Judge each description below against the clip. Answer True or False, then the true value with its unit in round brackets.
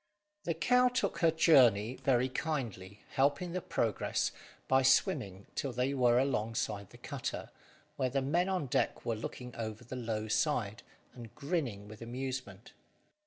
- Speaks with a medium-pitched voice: False (125 Hz)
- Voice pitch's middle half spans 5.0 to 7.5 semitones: False (4.4 semitones)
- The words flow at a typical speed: True (155 wpm)